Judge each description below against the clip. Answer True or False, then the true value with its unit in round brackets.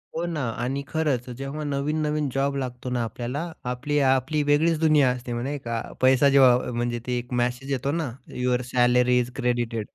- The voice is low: True (130 Hz)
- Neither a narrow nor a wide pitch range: True (3.0 semitones)